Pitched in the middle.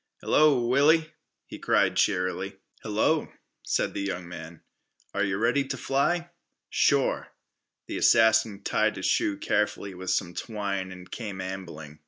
No: low, 100 Hz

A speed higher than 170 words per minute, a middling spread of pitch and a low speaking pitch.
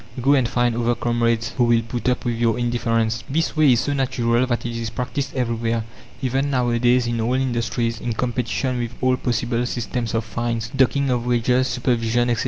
No: average, 190 wpm; narrow, 1.4 semitones; low, 120 Hz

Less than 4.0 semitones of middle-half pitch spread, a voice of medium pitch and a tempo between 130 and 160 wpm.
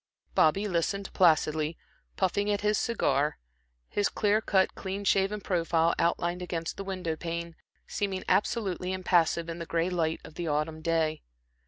Yes: average, 3.1 semitones; medium, 175 Hz; average, 150 wpm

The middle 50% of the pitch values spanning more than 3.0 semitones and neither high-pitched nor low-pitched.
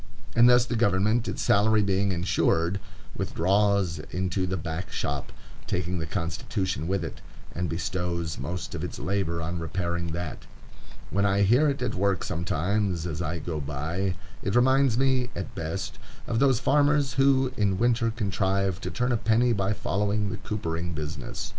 No: average, 4.6 semitones; very low, 95 Hz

